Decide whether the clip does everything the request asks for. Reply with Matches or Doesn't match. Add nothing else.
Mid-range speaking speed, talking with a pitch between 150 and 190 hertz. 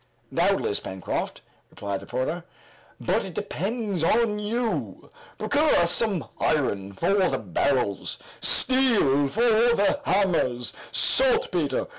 Doesn't match